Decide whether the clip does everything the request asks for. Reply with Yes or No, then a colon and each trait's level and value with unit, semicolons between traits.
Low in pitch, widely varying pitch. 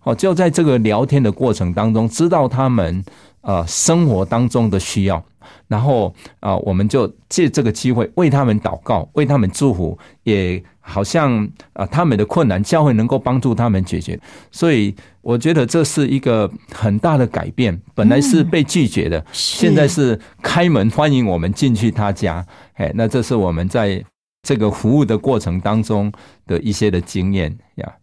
Yes: low, 110 Hz; wide, 5.8 semitones